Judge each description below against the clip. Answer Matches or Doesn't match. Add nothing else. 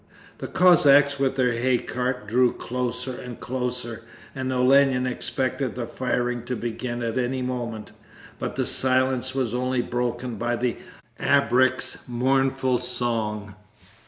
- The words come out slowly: Matches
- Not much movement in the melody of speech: Matches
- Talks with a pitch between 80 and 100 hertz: Doesn't match